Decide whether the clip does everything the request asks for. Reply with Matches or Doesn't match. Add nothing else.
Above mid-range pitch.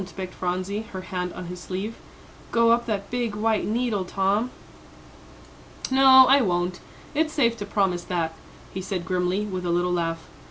Matches